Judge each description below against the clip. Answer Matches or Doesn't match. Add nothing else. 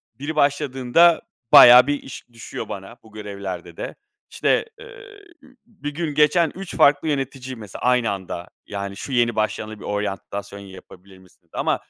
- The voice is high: Doesn't match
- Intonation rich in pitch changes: Matches